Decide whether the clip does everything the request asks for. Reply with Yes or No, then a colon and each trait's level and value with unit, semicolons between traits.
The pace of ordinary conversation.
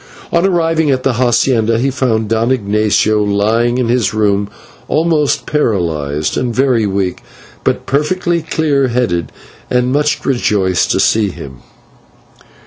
No: slow, 130 wpm